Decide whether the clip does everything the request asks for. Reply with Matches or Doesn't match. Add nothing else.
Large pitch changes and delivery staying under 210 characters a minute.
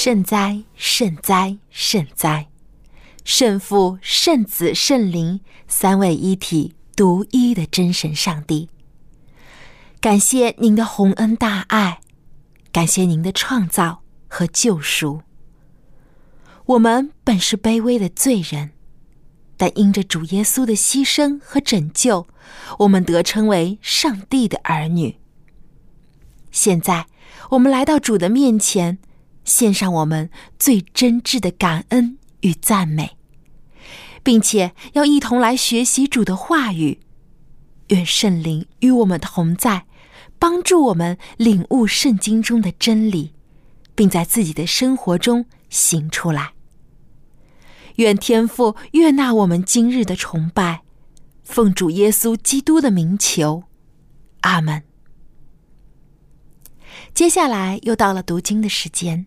Matches